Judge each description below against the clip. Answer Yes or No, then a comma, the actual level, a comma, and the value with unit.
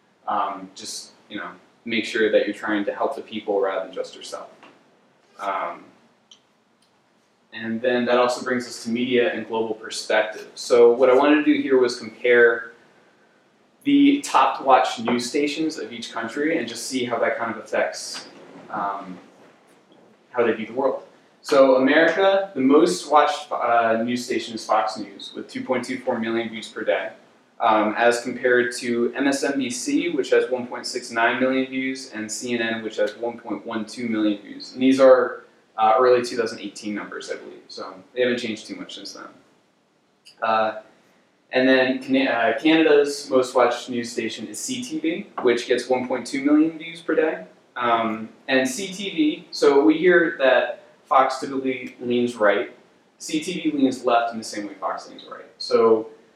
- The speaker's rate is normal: Yes, average, 160 wpm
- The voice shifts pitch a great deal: No, average, 4.8 semitones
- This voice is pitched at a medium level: No, low, 125 Hz